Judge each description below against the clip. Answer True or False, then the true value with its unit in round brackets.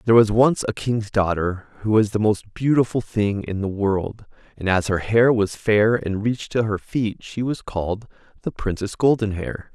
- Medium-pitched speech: False (105 Hz)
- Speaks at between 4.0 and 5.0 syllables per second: True (4.7 syllables/s)